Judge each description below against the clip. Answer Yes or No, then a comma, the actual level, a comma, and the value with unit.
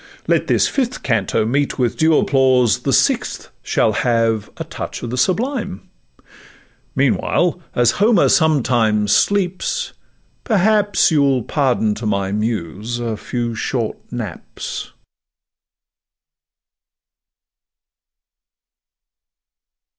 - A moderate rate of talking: No, slow, 95 wpm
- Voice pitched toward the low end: Yes, low, 125 Hz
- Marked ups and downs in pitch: Yes, wide, 6.4 semitones